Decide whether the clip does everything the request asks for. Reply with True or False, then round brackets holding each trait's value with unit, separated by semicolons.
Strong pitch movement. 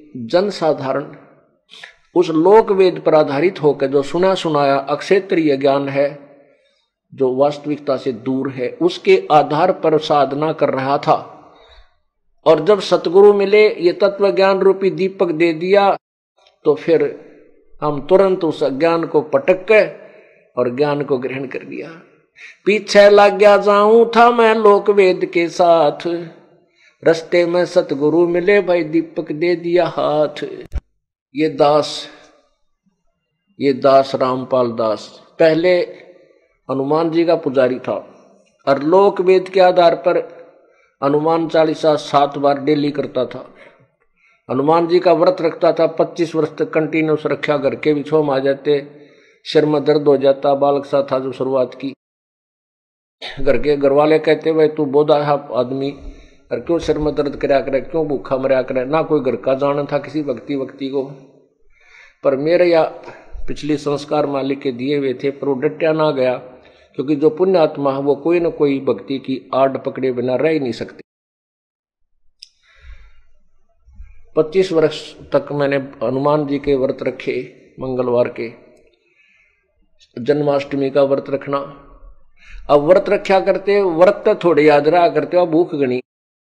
False (4.0 semitones)